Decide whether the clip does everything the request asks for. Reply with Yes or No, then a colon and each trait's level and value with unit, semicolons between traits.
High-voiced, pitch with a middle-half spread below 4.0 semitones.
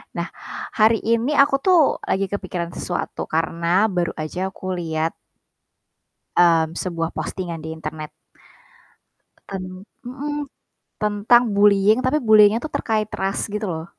No: high, 195 Hz; average, 4.8 semitones